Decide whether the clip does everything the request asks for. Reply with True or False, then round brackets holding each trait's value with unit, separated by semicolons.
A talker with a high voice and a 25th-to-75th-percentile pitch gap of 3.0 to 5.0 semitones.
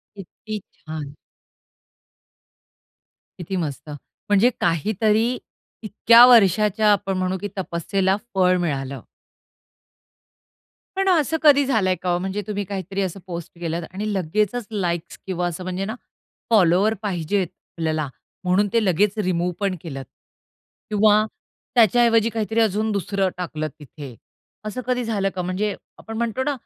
True (195 Hz; 3.6 semitones)